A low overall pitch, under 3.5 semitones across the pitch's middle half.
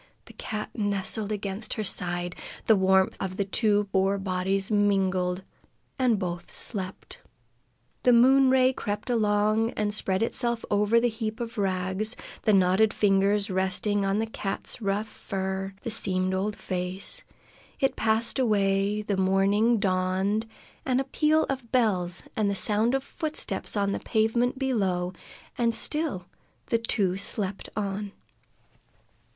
No: high, 205 Hz; average, 2.9 semitones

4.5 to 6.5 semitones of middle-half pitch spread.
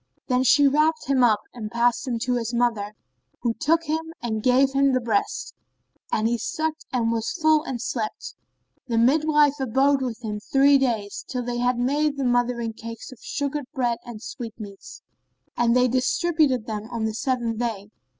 No: average, 3.3 semitones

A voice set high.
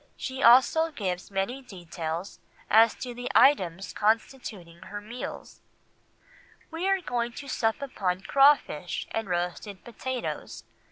Yes: high, 225 Hz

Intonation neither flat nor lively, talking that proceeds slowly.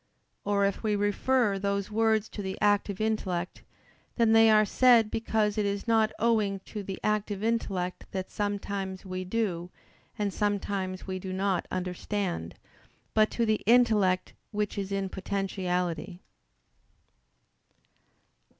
No: narrow, 2.3 semitones; slow, 130 wpm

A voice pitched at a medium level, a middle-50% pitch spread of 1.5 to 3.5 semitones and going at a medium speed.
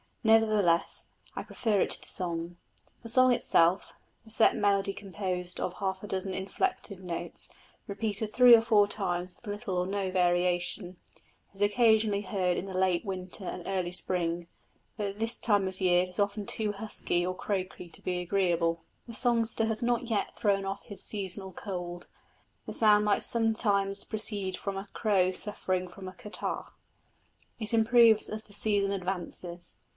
No: high, 195 Hz; average, 2.9 semitones; average, 170 wpm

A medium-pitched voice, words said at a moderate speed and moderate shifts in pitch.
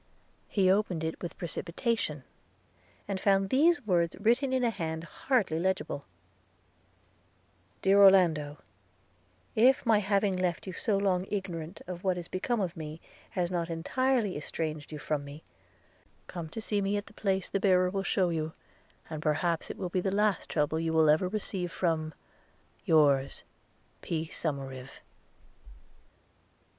Yes: medium, 180 Hz; average, 145 wpm; average, 3.8 semitones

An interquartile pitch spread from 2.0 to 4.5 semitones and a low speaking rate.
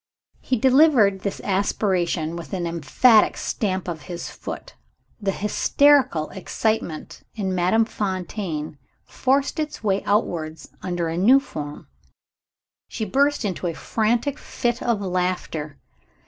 No: average, 5.1 semitones; slow, 120 wpm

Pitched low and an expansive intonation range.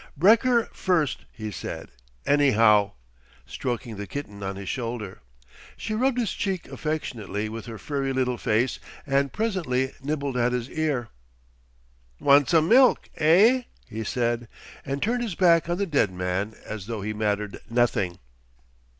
Yes: low, 130 Hz; wide, 7.2 semitones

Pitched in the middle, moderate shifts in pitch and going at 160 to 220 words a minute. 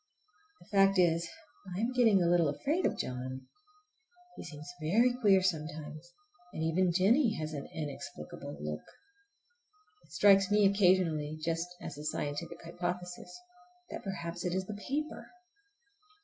No: medium, 175 Hz; average, 4.1 semitones; average, 140 wpm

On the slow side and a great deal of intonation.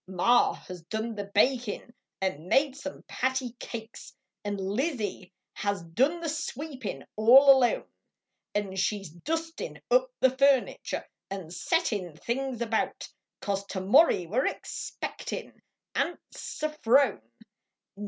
Yes: slow, 125 wpm; wide, 5.9 semitones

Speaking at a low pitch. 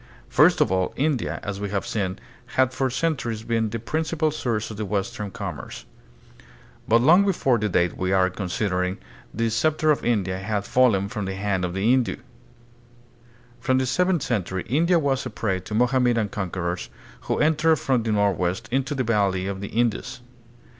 Yes: low, 110 Hz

